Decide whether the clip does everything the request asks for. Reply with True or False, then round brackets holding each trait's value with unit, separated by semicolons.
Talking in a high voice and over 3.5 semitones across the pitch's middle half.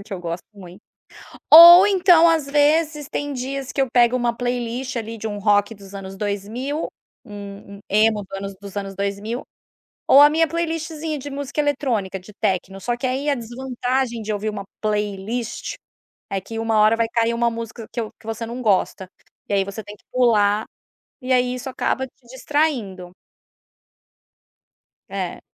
True (230 Hz; 4.7 semitones)